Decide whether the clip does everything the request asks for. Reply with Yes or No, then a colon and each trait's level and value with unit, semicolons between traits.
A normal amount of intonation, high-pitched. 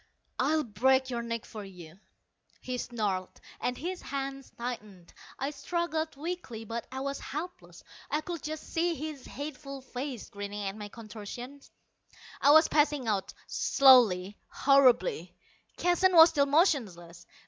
No: wide, 5.7 semitones; very high, 265 Hz